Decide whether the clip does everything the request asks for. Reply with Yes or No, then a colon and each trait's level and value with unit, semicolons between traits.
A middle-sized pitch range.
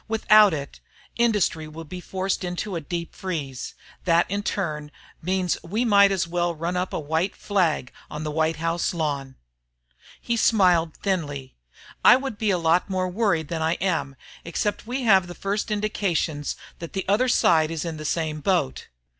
Yes: average, 3.9 semitones